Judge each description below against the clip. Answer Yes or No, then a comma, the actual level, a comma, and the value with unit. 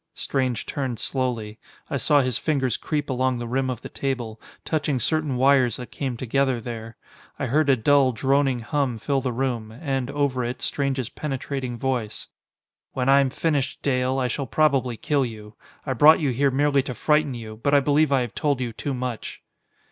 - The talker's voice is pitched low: Yes, low, 130 Hz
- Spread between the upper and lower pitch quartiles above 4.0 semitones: No, narrow, 2.6 semitones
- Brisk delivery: No, average, 190 wpm